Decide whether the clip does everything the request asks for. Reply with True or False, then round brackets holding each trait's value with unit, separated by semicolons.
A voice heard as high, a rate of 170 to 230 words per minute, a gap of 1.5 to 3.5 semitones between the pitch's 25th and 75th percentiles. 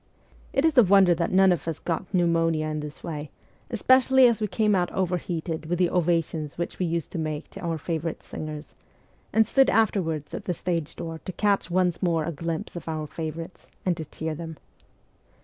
False (170 Hz; 200 wpm; 2.7 semitones)